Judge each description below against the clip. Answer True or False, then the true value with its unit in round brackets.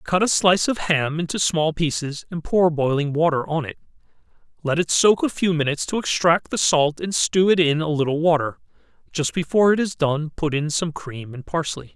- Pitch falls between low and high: True (160 Hz)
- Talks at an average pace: False (210 wpm)